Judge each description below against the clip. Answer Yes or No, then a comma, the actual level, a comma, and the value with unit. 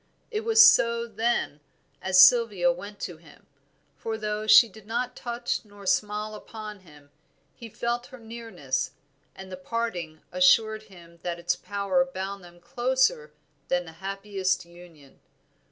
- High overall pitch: Yes, high, 205 Hz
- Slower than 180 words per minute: Yes, average, 145 wpm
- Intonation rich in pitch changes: No, average, 4.8 semitones